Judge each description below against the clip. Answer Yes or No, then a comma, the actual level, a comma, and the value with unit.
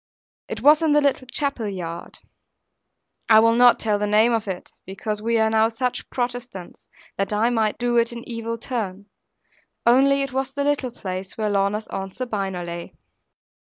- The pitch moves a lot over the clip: No, average, 3.5 semitones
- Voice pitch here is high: Yes, high, 225 Hz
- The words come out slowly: No, average, 175 wpm